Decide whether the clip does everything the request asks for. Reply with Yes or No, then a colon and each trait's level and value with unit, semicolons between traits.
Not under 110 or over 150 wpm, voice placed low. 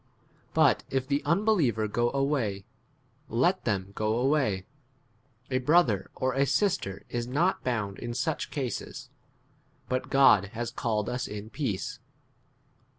Yes: slow, 135 wpm; low, 125 Hz